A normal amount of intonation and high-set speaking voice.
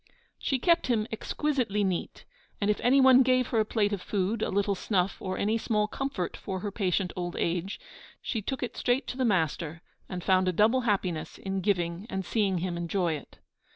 Yes: average, 4.1 semitones; high, 200 Hz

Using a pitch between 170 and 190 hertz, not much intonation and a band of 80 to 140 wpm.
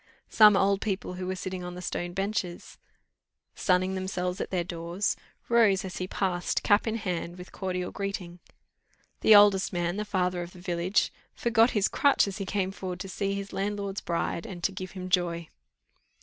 No: medium, 185 Hz; narrow, 1.9 semitones; average, 185 wpm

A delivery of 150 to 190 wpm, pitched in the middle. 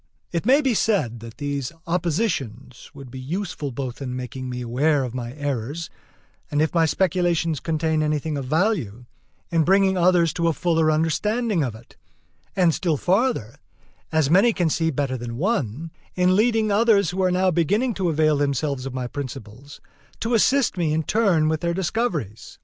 Yes: average, 175 wpm; medium, 160 Hz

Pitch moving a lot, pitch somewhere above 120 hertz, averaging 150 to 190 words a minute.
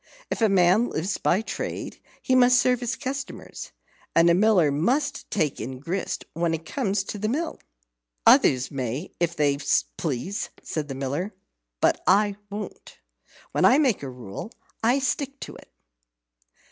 Yes: wide, 8.0 semitones; high, 190 Hz; average, 160 wpm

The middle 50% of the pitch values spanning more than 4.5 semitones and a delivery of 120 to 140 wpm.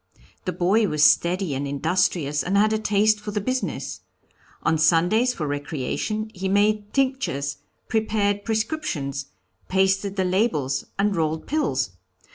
Yes: wide, 5.6 semitones; slow, 135 wpm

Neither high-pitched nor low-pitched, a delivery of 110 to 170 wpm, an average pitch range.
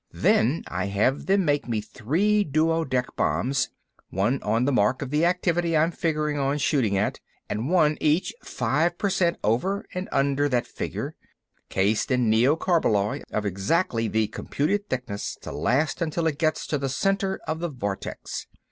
No: medium, 145 Hz; average, 155 wpm; wide, 6.6 semitones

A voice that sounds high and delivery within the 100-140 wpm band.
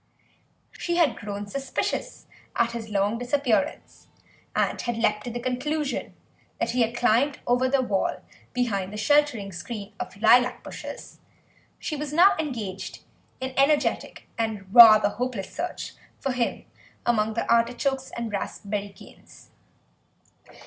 Yes: high, 235 Hz; slow, 135 wpm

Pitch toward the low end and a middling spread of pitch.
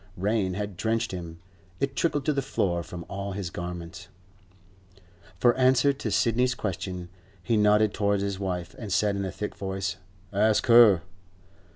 Yes: low, 100 Hz; average, 3.9 semitones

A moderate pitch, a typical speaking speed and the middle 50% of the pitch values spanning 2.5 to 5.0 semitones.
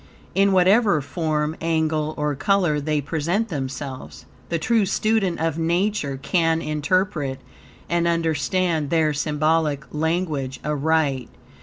No: medium, 160 Hz; slow, 115 wpm; average, 2.9 semitones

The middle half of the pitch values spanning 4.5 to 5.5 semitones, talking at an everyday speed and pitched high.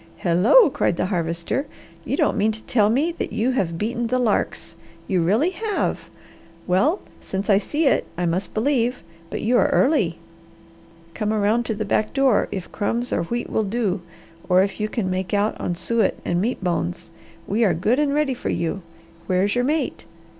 Yes: average, 5.0 semitones; average, 190 wpm; high, 215 Hz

